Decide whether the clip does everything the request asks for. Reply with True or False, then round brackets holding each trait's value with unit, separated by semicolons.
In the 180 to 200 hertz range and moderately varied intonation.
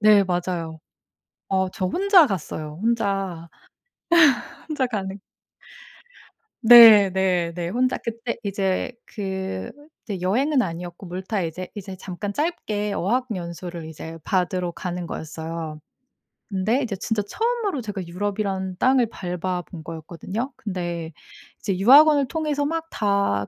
True (190 Hz; 4.7 semitones)